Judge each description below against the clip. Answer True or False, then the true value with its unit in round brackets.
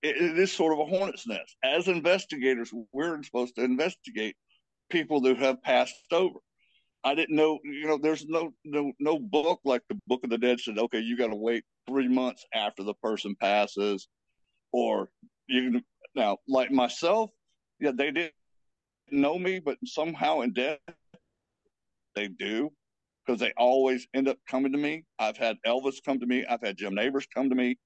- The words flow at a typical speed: True (180 wpm)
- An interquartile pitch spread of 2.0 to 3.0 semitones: False (4.4 semitones)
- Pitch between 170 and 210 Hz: False (135 Hz)